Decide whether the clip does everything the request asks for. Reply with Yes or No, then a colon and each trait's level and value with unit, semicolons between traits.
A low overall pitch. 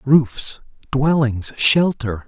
Yes: low, 130 Hz